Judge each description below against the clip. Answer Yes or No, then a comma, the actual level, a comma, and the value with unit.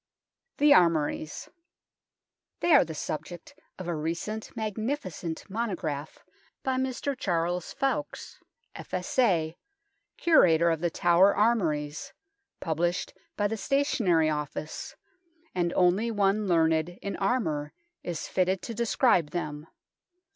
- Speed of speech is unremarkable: No, slow, 110 wpm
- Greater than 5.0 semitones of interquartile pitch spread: Yes, wide, 5.4 semitones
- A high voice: No, medium, 180 Hz